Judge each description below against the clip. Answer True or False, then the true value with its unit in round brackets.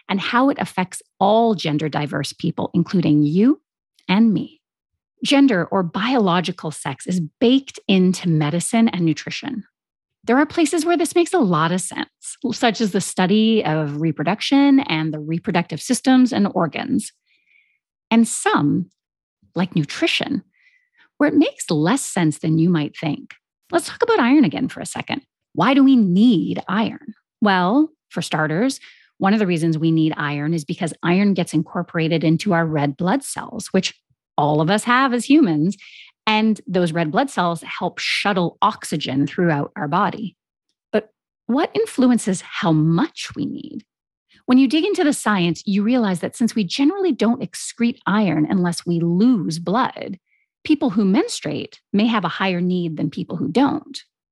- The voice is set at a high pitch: True (195 Hz)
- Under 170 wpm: True (160 wpm)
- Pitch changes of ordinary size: False (7.1 semitones)